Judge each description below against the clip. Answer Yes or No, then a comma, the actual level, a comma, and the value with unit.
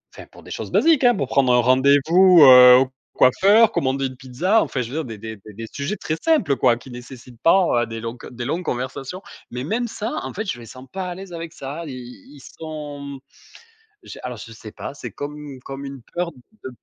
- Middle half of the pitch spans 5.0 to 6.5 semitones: Yes, average, 5.3 semitones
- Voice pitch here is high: No, low, 135 Hz